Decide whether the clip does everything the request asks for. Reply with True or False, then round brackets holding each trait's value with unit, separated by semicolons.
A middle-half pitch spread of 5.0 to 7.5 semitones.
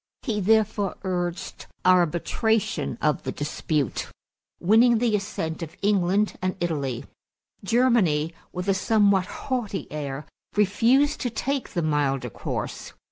True (5.5 semitones)